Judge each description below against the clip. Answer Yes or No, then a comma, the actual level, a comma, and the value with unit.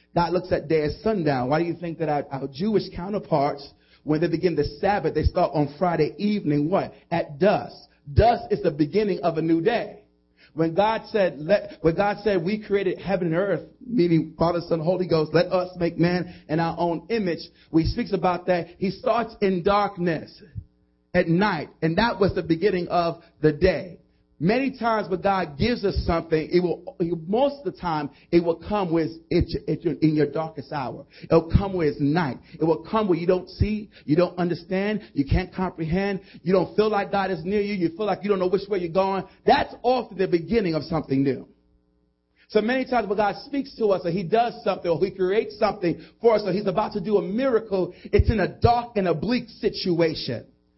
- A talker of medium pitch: Yes, medium, 180 Hz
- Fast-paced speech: Yes, fast, 210 wpm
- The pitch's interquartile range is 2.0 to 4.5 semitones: Yes, average, 4.0 semitones